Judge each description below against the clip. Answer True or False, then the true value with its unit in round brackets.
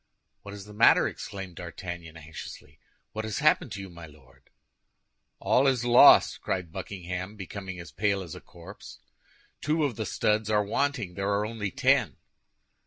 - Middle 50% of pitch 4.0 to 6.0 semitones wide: False (3.6 semitones)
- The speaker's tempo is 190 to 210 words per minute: False (165 wpm)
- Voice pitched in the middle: False (100 Hz)